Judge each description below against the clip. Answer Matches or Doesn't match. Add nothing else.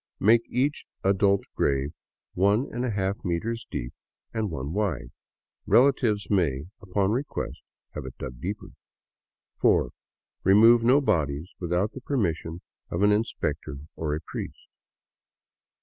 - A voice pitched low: Matches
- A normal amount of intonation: Doesn't match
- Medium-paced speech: Doesn't match